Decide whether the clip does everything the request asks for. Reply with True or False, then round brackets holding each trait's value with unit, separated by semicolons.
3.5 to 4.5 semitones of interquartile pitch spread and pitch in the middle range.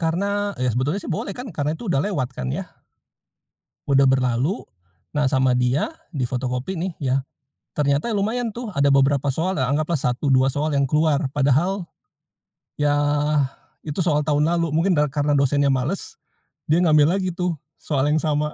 True (3.9 semitones; 145 Hz)